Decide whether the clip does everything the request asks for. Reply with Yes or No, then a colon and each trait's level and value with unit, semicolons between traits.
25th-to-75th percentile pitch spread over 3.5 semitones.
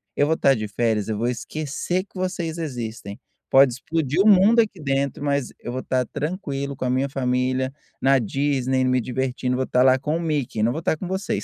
Yes: average, 3.9 semitones